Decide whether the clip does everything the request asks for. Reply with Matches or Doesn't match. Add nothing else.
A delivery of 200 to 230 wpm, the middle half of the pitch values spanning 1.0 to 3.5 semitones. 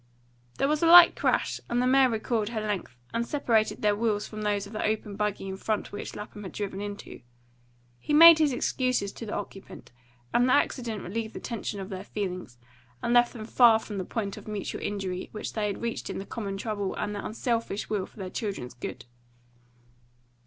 Matches